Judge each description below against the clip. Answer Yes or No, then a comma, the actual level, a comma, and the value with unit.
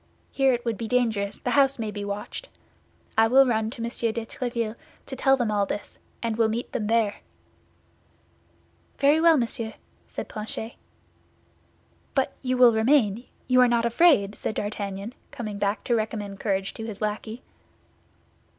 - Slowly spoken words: No, average, 160 wpm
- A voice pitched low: No, high, 225 Hz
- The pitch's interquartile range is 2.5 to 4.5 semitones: Yes, average, 2.9 semitones